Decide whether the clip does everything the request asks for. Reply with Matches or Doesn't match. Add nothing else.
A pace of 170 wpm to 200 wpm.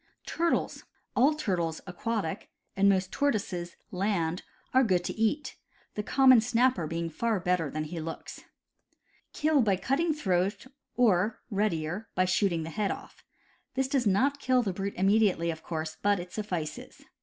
Doesn't match